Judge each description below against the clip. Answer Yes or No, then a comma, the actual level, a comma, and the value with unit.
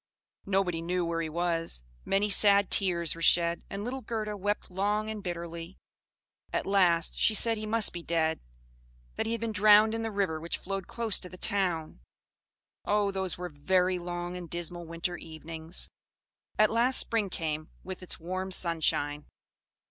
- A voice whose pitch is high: No, medium, 180 Hz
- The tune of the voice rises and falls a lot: No, average, 3.5 semitones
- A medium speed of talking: Yes, average, 170 wpm